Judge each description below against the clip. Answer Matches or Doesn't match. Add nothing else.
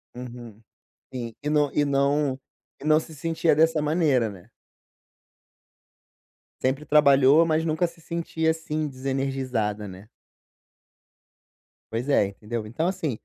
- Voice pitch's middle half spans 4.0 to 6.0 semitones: Matches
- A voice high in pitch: Doesn't match